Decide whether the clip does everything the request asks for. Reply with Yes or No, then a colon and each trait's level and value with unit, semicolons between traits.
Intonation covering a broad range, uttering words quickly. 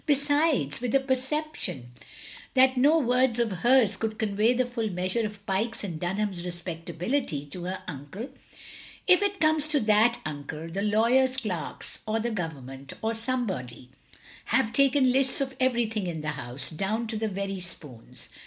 No: wide, 6.8 semitones; average, 165 wpm